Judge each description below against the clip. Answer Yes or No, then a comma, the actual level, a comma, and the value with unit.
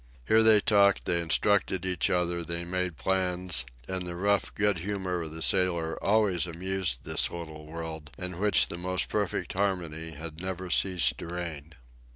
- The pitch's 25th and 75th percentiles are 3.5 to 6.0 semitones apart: No, narrow, 2.4 semitones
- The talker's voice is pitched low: Yes, very low, 90 Hz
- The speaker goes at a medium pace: Yes, average, 170 wpm